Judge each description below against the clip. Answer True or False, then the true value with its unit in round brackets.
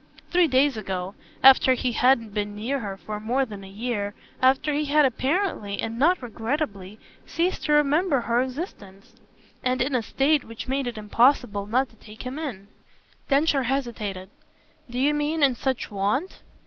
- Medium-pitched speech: False (250 Hz)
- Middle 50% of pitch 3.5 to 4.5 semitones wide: False (4.9 semitones)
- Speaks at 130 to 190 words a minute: True (170 wpm)